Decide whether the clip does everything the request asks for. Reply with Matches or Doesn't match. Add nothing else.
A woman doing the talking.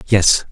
Doesn't match